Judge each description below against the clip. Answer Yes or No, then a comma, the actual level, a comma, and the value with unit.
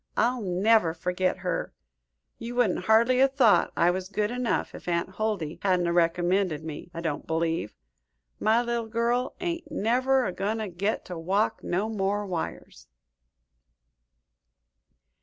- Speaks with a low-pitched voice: No, high, 200 Hz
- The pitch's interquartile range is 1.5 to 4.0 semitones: No, average, 4.8 semitones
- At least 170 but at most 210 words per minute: No, average, 145 wpm